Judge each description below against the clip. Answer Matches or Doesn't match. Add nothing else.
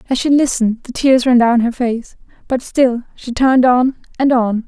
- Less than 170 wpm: Doesn't match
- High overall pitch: Matches